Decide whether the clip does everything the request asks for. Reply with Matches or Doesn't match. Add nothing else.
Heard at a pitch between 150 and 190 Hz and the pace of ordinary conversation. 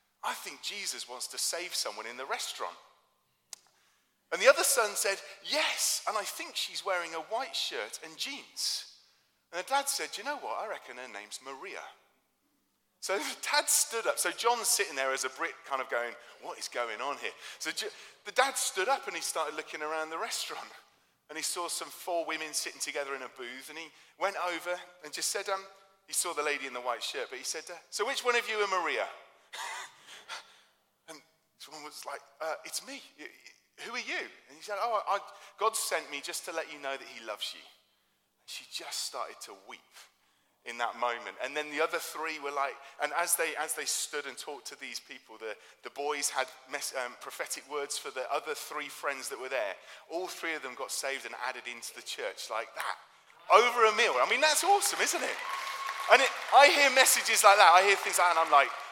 Doesn't match